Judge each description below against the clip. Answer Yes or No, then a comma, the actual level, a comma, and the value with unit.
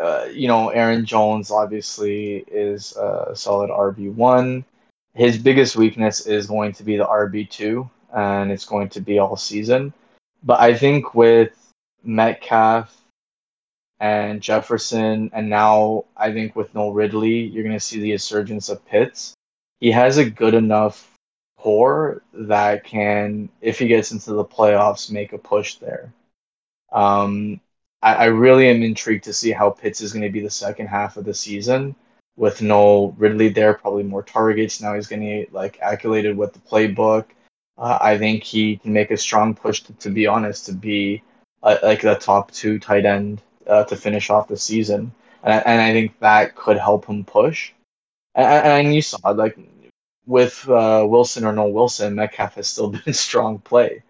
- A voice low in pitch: Yes, low, 105 Hz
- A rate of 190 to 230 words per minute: No, average, 175 wpm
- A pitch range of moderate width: No, narrow, 1.5 semitones